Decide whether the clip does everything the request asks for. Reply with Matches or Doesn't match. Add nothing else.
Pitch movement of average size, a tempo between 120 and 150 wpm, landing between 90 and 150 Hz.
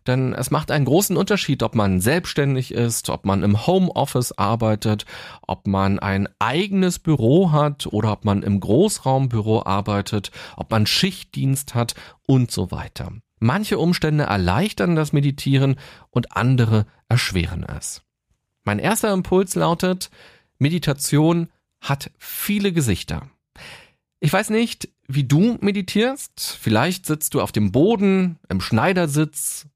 Doesn't match